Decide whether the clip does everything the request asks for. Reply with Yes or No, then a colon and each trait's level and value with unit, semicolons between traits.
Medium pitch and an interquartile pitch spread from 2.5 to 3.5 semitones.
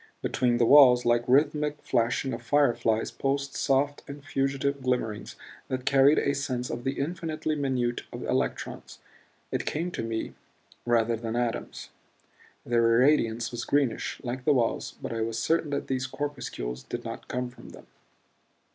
No: low, 130 Hz; average, 3.1 semitones